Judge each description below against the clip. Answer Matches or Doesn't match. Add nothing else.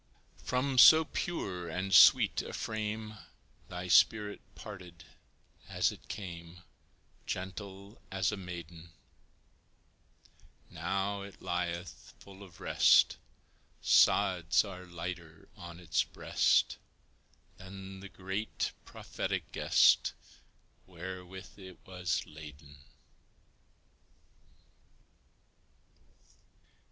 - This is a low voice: Matches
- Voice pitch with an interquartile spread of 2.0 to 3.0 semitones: Matches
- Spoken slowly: Matches